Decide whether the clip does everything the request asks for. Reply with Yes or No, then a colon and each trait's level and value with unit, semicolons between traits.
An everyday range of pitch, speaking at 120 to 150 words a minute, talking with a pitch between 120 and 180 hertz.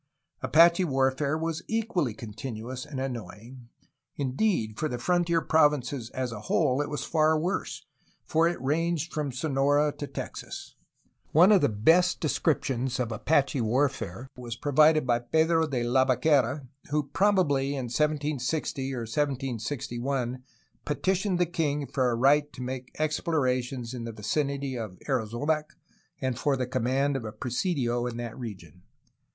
Yes: average, 3.9 semitones; average, 145 wpm; low, 135 Hz